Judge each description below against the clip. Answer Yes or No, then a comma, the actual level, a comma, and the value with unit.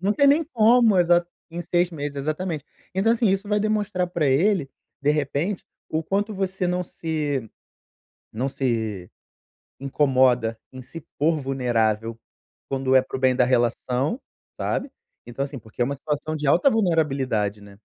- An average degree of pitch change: No, wide, 6.1 semitones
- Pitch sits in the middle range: Yes, medium, 150 Hz